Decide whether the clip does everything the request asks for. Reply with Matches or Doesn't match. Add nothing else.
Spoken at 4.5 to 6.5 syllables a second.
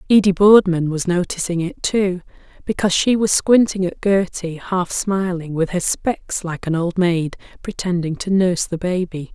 Matches